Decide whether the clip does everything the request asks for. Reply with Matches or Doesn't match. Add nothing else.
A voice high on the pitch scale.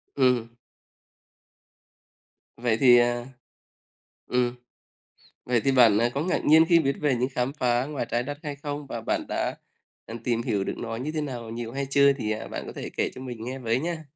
Doesn't match